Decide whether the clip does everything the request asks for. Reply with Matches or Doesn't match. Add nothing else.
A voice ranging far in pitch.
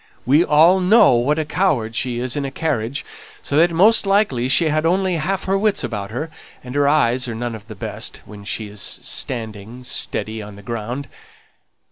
Matches